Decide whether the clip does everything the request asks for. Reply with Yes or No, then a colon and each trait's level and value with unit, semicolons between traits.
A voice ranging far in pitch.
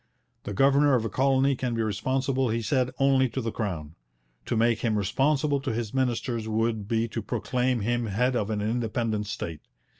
No: average, 3.3 semitones